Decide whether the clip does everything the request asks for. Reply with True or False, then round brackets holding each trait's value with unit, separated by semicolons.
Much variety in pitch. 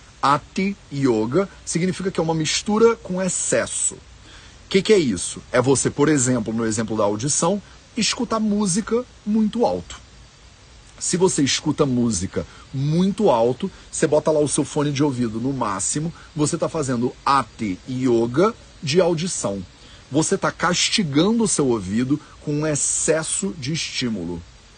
True (7.1 semitones)